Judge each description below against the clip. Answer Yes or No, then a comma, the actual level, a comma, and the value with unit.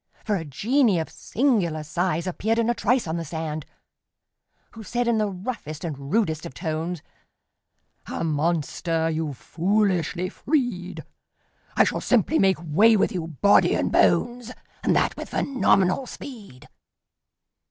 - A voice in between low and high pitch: Yes, medium, 180 Hz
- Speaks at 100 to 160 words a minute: Yes, average, 140 wpm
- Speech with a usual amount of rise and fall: No, wide, 5.8 semitones